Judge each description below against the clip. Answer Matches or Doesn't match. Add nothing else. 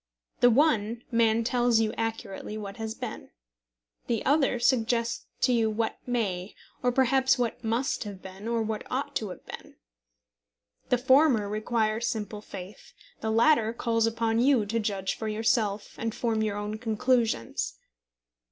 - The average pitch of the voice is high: Matches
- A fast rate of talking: Doesn't match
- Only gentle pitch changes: Matches